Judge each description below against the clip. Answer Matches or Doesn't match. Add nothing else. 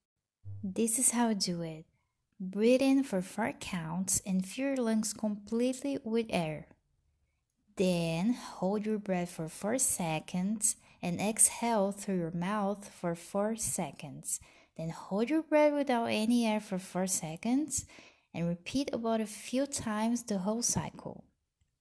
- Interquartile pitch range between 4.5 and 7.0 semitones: Matches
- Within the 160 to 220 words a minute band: Doesn't match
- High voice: Matches